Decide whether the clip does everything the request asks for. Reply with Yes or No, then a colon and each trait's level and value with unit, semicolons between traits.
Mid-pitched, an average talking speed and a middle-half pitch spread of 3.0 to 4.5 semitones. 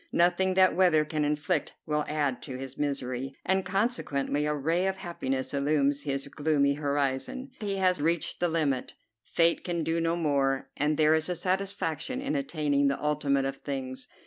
Yes: medium, 150 Hz; average, 170 wpm; average, 4.0 semitones